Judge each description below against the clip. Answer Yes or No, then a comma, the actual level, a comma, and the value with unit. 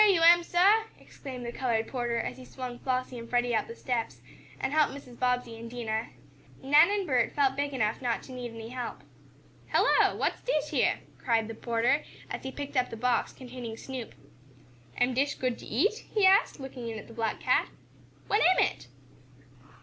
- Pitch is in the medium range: No, very high, 250 Hz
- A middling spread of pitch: Yes, average, 3.4 semitones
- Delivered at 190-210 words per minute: Yes, average, 195 wpm